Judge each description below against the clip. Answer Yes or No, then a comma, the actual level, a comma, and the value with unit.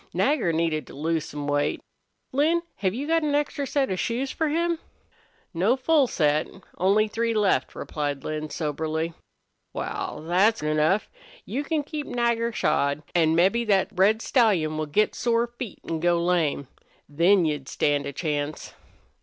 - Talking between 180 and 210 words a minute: No, average, 160 wpm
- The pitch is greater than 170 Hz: Yes, medium, 185 Hz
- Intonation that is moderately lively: No, wide, 7.5 semitones